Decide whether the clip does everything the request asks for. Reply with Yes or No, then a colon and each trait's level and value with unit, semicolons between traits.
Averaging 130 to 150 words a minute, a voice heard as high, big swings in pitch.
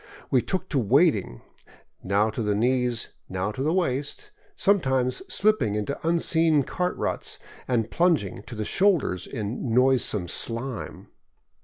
No: slow, 135 wpm; low, 125 Hz; wide, 7.1 semitones